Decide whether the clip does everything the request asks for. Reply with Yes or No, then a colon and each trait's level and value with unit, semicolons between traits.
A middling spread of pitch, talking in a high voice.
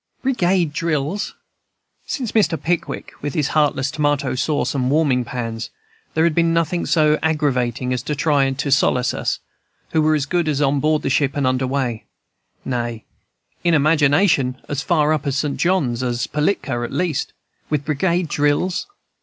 No: average, 3.4 semitones; medium, 145 Hz